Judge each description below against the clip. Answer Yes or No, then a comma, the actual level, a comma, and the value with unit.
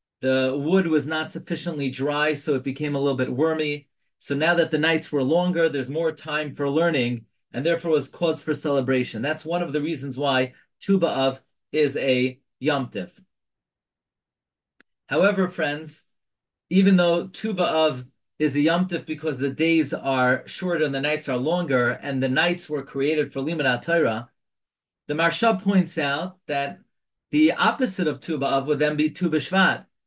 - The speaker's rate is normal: Yes, average, 160 wpm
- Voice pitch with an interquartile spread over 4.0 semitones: No, average, 3.7 semitones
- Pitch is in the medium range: Yes, medium, 150 Hz